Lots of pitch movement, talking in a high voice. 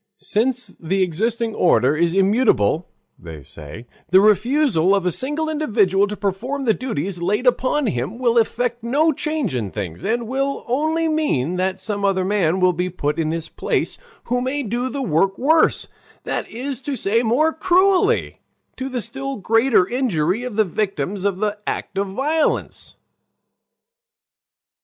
Yes: wide, 6.3 semitones; high, 215 Hz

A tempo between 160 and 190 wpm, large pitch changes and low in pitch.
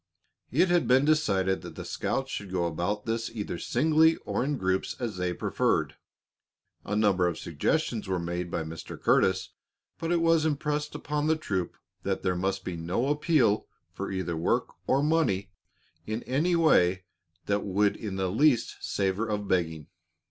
Yes: average, 170 wpm; wide, 8.1 semitones; low, 105 Hz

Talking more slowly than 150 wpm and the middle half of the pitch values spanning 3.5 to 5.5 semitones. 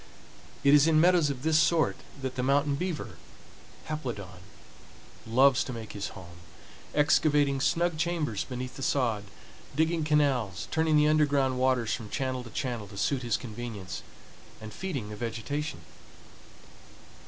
Yes: average, 140 wpm; average, 4.7 semitones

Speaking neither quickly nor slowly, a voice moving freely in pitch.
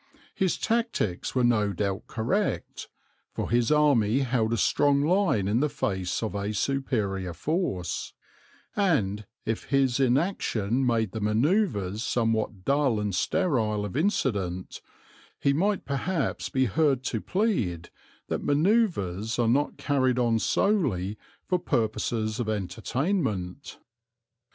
No: slow, 125 wpm; wide, 6.0 semitones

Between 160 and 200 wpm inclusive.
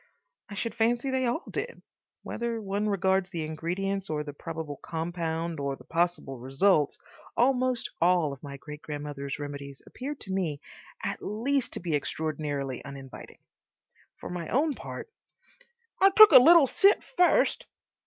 No: average, 150 wpm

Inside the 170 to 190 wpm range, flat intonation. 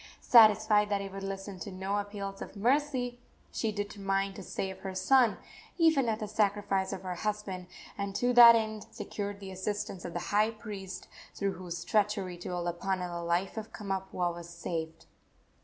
Yes: average, 175 wpm; narrow, 2.3 semitones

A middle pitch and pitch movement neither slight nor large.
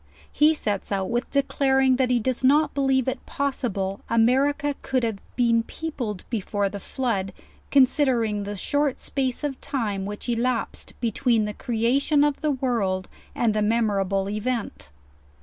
No: high, 240 Hz; average, 4.3 semitones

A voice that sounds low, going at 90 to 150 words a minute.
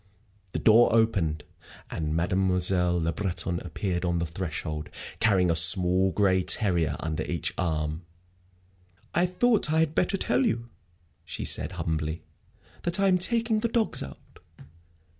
Yes: very low, 90 Hz; average, 140 wpm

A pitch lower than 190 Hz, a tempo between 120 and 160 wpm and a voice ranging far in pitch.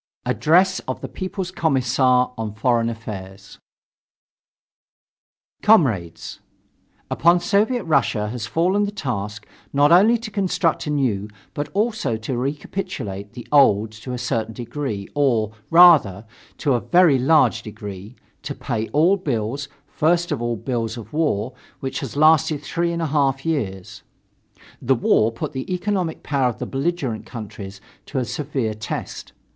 Yes: low, 135 Hz; average, 150 wpm; wide, 6.6 semitones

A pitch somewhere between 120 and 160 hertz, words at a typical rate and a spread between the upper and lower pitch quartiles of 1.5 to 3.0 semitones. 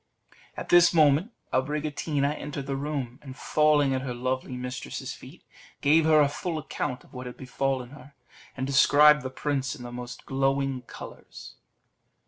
Yes: medium, 140 Hz; average, 160 wpm; narrow, 2.5 semitones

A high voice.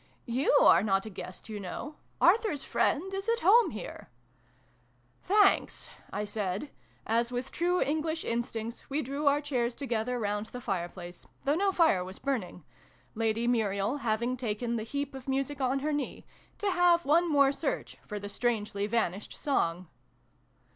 Yes: high, 245 Hz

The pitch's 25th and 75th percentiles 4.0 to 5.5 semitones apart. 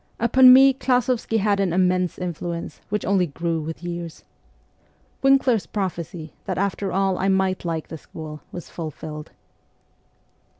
No: average, 3.6 semitones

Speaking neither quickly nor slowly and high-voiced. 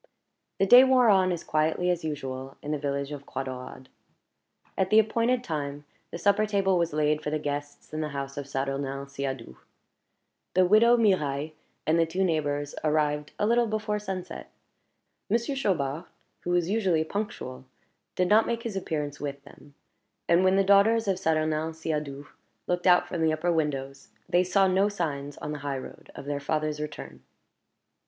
No: average, 175 wpm; medium, 160 Hz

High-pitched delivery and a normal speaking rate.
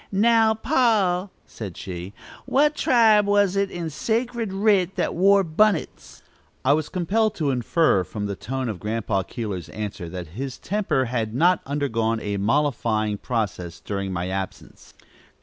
No: medium, 140 Hz; average, 150 wpm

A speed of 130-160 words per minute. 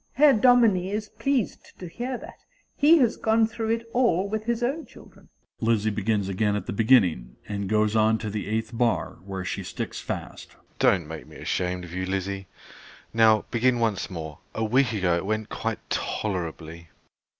No: average, 185 wpm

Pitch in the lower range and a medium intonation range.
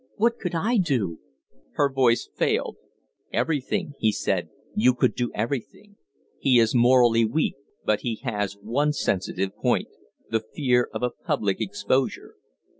Yes: low, 125 Hz; average, 4.8 semitones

